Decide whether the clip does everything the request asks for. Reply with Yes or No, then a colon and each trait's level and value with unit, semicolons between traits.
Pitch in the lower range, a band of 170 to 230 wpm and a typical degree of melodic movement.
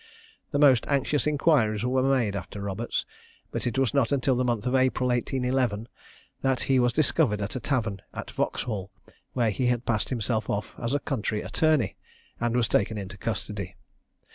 Yes: low, 120 Hz; average, 175 wpm; average, 3.7 semitones